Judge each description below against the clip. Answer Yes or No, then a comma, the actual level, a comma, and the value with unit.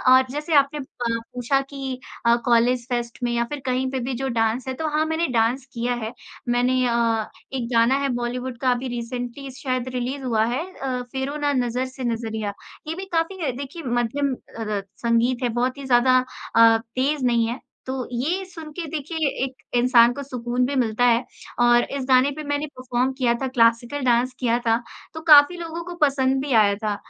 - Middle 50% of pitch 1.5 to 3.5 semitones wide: Yes, average, 2.8 semitones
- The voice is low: No, very high, 255 Hz